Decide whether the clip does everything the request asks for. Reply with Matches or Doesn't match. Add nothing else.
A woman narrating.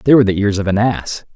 Doesn't match